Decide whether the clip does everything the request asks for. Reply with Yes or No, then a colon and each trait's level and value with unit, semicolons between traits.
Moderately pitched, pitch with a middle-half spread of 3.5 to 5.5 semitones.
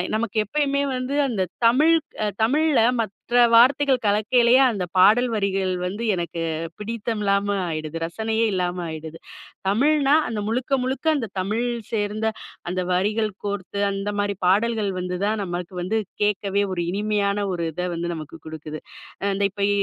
No: high, 205 Hz; average, 3.9 semitones